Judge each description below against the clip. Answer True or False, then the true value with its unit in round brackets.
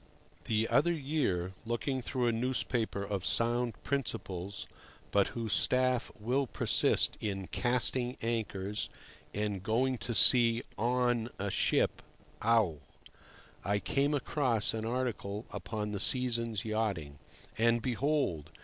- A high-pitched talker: False (115 Hz)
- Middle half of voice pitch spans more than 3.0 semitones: True (3.6 semitones)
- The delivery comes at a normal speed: False (120 wpm)